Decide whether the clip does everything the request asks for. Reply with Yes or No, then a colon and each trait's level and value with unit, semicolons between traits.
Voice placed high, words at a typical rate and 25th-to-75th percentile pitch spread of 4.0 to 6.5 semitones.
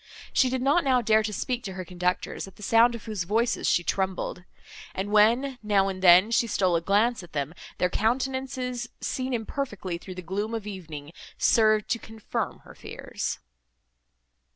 Yes: high, 210 Hz; average, 175 wpm; average, 4.4 semitones